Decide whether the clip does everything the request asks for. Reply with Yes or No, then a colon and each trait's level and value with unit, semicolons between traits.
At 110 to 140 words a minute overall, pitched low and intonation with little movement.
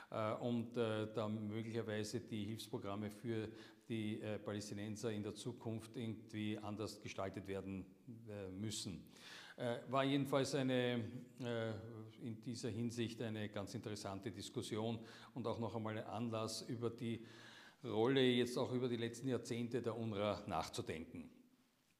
Yes: average, 135 wpm; low, 115 Hz; narrow, 2.2 semitones